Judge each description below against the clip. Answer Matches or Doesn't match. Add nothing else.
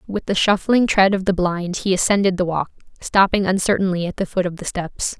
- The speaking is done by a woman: Matches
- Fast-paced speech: Matches